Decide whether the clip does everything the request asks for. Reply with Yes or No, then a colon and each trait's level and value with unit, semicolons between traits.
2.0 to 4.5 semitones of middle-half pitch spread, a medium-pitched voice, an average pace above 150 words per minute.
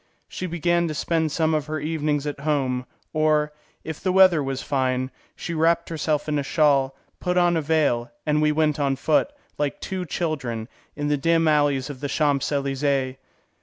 Yes: narrow, 2.6 semitones; medium, 150 Hz; average, 185 wpm